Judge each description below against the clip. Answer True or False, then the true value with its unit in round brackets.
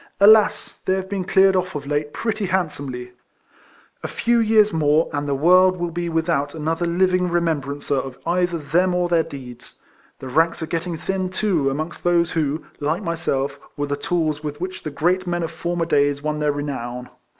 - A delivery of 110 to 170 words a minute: False (185 wpm)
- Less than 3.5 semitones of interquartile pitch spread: False (3.8 semitones)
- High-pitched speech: False (165 Hz)